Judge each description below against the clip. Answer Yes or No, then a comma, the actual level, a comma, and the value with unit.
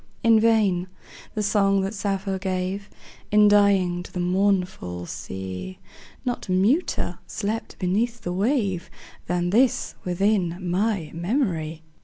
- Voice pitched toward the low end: No, high, 195 Hz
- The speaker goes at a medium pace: No, slow, 120 wpm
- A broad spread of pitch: No, average, 3.0 semitones